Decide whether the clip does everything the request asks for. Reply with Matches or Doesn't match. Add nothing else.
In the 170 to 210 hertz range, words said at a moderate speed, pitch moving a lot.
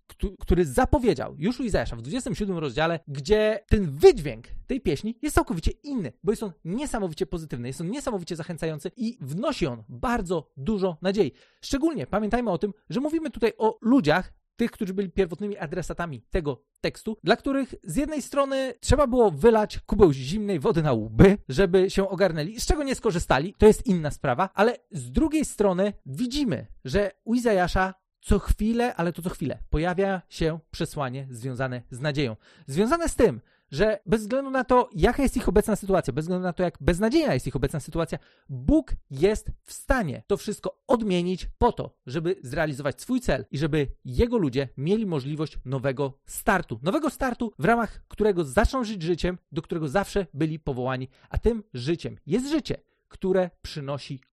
Doesn't match